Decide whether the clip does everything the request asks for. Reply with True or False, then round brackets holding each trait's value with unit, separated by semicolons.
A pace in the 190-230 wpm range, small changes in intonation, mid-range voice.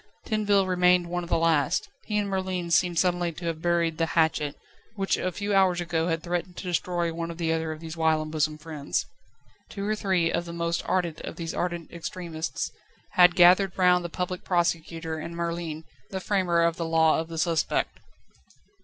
True (195 wpm; 1.8 semitones; 170 Hz)